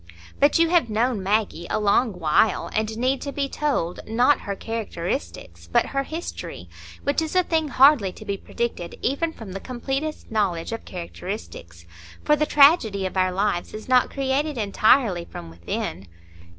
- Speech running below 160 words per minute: No, average, 165 wpm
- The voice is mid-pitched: No, high, 225 Hz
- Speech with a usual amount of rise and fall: No, wide, 6.9 semitones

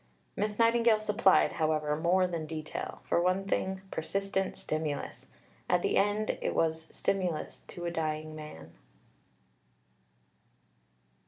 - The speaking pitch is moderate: Yes, medium, 170 Hz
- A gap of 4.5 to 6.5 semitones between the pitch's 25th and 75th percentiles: No, average, 4.0 semitones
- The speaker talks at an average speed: No, slow, 115 wpm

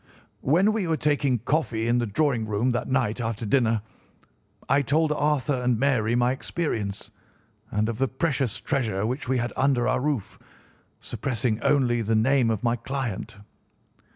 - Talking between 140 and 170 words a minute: Yes, average, 160 wpm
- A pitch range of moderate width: Yes, average, 3.7 semitones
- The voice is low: Yes, low, 125 Hz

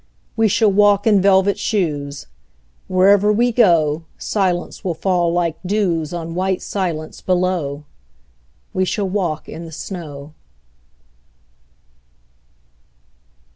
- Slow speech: Yes, slow, 105 wpm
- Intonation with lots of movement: No, average, 3.6 semitones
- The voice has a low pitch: No, medium, 185 Hz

